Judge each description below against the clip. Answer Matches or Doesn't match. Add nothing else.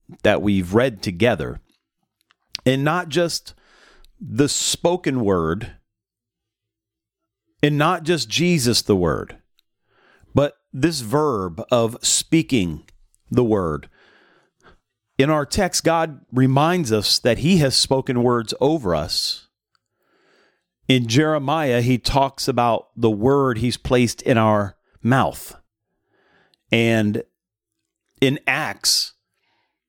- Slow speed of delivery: Matches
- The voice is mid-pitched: Doesn't match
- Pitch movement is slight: Doesn't match